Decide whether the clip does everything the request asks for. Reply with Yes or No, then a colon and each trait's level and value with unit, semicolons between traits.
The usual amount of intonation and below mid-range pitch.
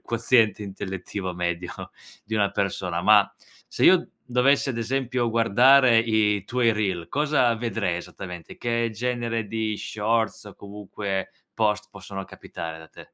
Yes: average, 3.2 semitones; low, 110 Hz